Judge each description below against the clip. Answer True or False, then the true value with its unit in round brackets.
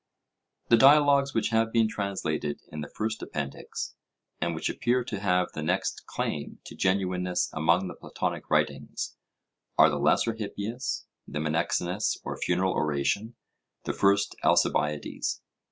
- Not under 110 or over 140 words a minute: True (135 wpm)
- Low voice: True (95 Hz)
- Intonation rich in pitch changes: True (6.0 semitones)